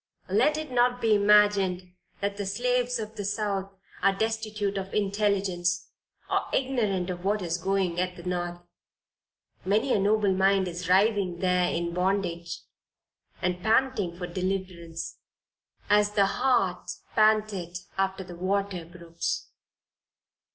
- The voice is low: No, high, 195 Hz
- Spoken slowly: Yes, slow, 130 wpm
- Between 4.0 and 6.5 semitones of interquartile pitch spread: No, average, 2.7 semitones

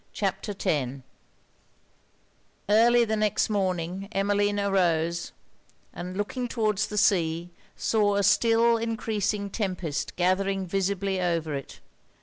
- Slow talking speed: Yes, slow, 110 wpm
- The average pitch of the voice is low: No, high, 195 Hz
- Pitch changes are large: No, average, 3.0 semitones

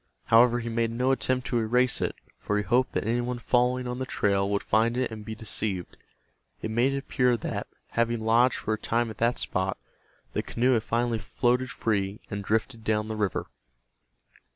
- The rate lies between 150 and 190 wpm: No, average, 200 wpm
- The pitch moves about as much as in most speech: No, narrow, 2.3 semitones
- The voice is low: Yes, low, 115 Hz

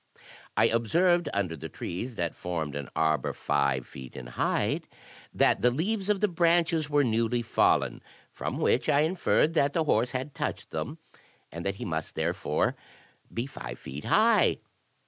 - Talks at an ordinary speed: Yes, average, 165 wpm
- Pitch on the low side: Yes, low, 120 Hz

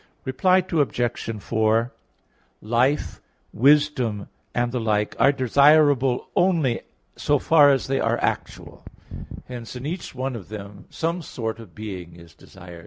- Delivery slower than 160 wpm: Yes, slow, 135 wpm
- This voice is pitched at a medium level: No, low, 125 Hz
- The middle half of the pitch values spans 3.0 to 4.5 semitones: No, average, 4.9 semitones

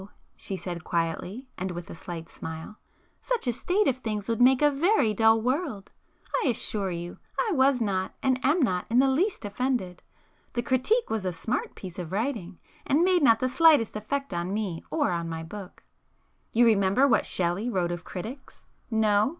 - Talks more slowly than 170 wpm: No, average, 185 wpm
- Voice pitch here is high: Yes, high, 220 Hz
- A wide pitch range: Yes, wide, 6.5 semitones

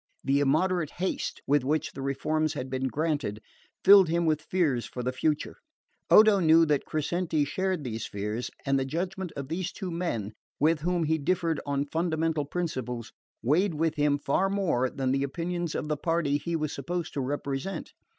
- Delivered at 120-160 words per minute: No, average, 180 wpm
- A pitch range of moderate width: Yes, average, 3.8 semitones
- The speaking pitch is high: No, medium, 155 Hz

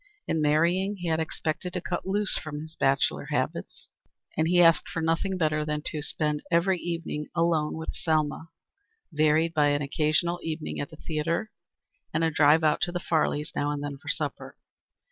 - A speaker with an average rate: Yes, average, 185 wpm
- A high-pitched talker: No, medium, 160 Hz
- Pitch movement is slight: Yes, narrow, 2.1 semitones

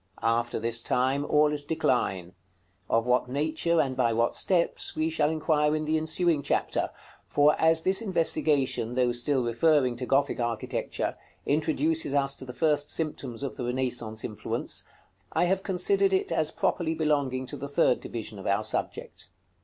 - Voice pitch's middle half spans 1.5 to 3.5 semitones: No, average, 4.5 semitones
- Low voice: No, medium, 145 Hz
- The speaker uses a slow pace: No, average, 165 wpm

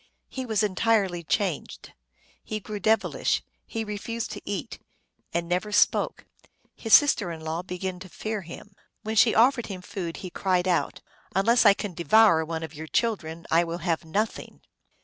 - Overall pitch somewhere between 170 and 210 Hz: Yes, high, 190 Hz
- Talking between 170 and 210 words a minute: Yes, average, 180 wpm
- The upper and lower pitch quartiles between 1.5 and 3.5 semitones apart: No, average, 4.2 semitones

